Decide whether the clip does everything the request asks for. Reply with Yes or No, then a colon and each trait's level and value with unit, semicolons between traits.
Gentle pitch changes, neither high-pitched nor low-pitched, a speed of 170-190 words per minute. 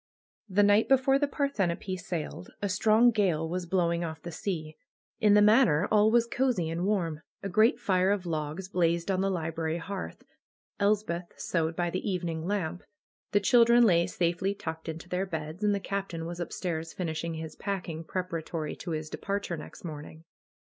No: average, 3.7 semitones; medium, 180 Hz; average, 180 wpm